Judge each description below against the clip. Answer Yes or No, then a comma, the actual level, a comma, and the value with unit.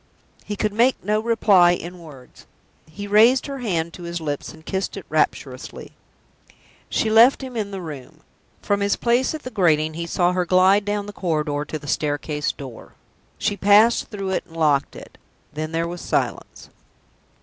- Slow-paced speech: No, average, 180 wpm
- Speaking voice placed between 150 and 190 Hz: Yes, medium, 185 Hz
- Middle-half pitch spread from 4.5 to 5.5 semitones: Yes, average, 4.8 semitones